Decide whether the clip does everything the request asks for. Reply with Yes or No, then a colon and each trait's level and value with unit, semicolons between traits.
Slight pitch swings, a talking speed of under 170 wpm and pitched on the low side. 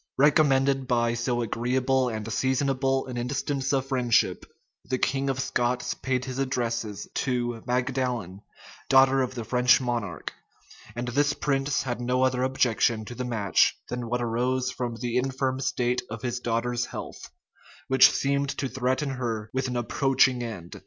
Yes: narrow, 1.8 semitones; average, 155 wpm; low, 125 Hz